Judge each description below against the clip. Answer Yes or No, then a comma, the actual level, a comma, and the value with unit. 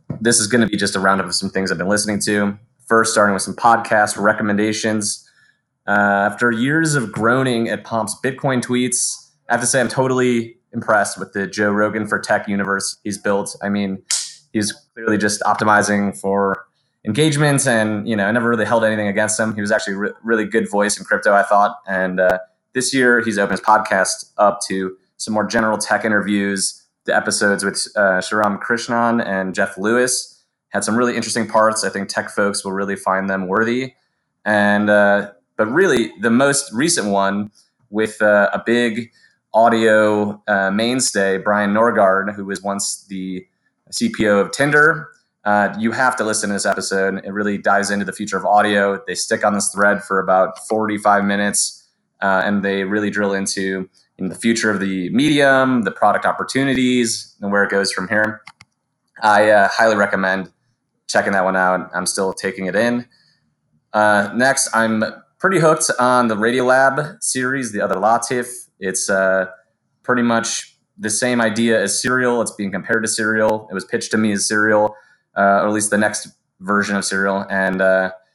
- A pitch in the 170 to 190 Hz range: No, low, 105 Hz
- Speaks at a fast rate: No, average, 185 wpm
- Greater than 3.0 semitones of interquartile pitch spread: No, average, 2.7 semitones